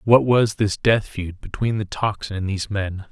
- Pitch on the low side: Yes, low, 100 Hz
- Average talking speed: No, fast, 210 wpm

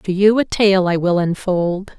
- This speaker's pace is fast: Yes, fast, 210 wpm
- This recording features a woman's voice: Yes, female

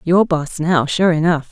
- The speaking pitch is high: No, medium, 165 Hz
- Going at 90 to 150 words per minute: No, average, 200 wpm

